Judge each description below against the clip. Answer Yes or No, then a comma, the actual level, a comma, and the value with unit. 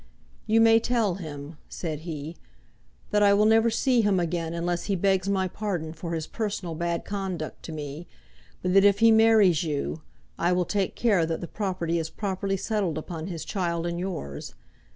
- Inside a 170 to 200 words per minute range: Yes, average, 185 wpm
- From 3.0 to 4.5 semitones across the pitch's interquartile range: Yes, average, 3.6 semitones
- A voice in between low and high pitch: Yes, medium, 180 Hz